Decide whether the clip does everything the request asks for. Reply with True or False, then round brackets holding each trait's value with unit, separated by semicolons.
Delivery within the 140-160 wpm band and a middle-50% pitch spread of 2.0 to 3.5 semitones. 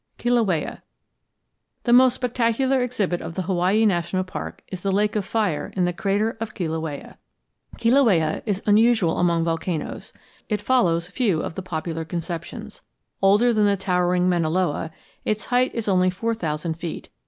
False (155 wpm; 4.6 semitones)